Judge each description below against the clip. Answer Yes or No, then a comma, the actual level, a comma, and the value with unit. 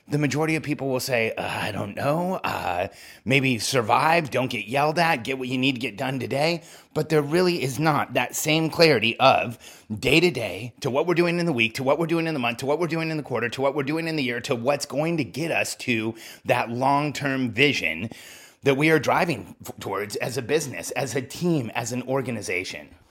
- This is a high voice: No, medium, 140 Hz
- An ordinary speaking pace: No, fast, 235 wpm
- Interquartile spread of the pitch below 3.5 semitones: No, average, 4.0 semitones